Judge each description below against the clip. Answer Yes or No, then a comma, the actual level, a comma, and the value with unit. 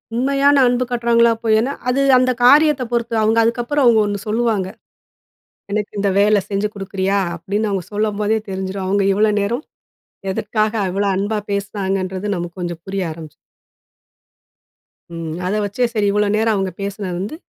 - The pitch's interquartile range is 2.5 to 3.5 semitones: Yes, average, 3.2 semitones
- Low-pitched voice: No, high, 210 Hz